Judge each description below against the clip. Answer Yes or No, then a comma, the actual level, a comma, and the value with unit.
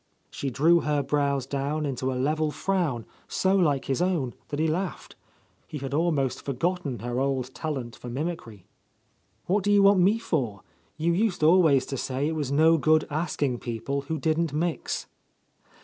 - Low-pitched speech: No, medium, 150 Hz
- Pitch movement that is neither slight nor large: Yes, average, 4.0 semitones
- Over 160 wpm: Yes, average, 170 wpm